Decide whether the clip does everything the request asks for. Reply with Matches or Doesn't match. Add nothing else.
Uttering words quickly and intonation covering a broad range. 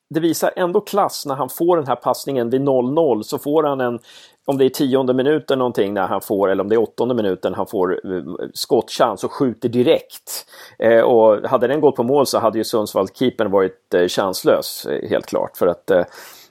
Matches